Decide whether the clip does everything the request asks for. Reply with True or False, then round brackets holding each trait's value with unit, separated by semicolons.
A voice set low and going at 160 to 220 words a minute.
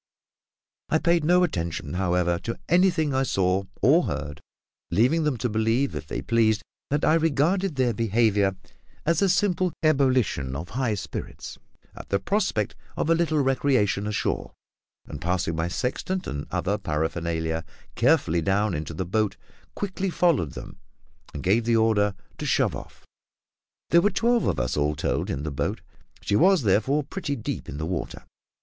True (110 Hz; 165 wpm)